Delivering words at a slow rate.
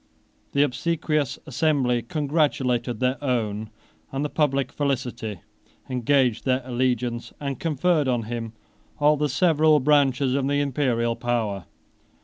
Yes: slow, 125 wpm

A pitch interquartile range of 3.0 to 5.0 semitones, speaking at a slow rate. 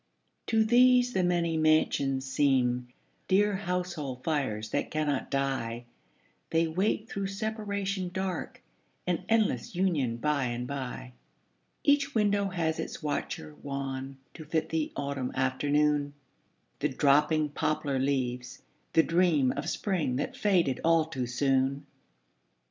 No: wide, 5.4 semitones; slow, 125 wpm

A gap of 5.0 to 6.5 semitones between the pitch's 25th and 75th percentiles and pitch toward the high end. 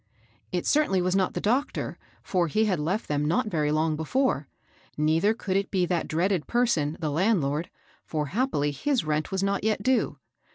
No: wide, 5.6 semitones; medium, 180 Hz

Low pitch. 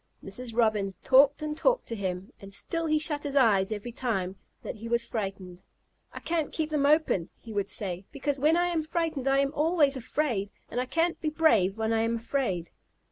No: very high, 255 Hz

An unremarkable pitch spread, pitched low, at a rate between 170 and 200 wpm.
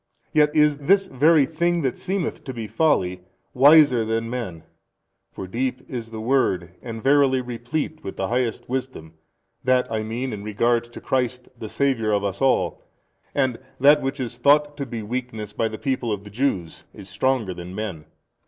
Yes: average, 4.2 semitones; low, 125 Hz; average, 180 wpm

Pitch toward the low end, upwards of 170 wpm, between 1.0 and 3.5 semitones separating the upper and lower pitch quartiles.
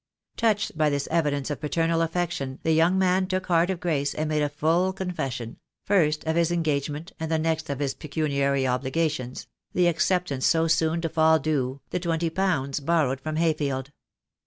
No: medium, 160 Hz; average, 190 wpm; average, 3.1 semitones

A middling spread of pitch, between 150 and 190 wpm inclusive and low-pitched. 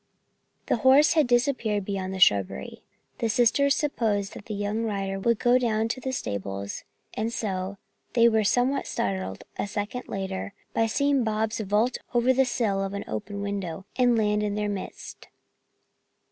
No: average, 3.6 semitones; average, 165 wpm; high, 215 Hz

